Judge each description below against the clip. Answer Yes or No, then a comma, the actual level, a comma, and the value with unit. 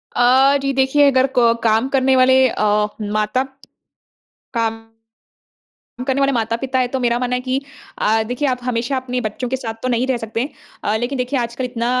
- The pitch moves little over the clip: Yes, narrow, 2.1 semitones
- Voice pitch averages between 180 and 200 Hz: No, very high, 250 Hz